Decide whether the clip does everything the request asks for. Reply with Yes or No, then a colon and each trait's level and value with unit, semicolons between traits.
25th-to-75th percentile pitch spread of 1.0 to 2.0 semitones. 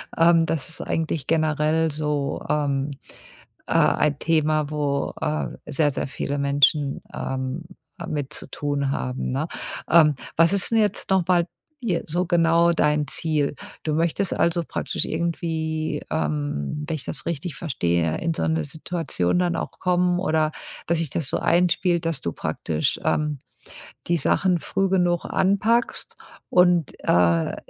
No: average, 2.9 semitones